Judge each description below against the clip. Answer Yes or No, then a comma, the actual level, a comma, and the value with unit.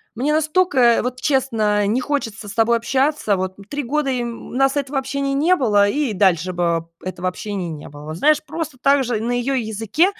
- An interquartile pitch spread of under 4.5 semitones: No, wide, 5.4 semitones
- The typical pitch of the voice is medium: No, high, 245 Hz